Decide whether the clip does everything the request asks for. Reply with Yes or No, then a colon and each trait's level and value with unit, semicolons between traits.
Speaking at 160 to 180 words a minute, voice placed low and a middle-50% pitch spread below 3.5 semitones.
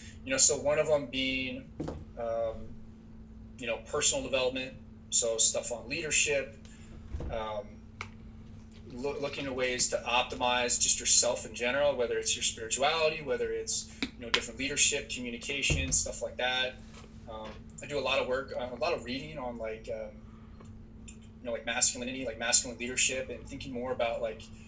Yes: average, 165 wpm; low, 115 Hz; average, 2.7 semitones